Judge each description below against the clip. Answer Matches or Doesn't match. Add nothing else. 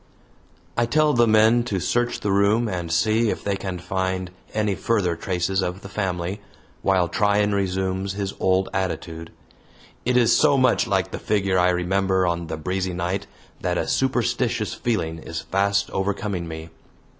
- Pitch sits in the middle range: Doesn't match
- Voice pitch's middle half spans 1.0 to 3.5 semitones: Matches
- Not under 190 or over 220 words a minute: Doesn't match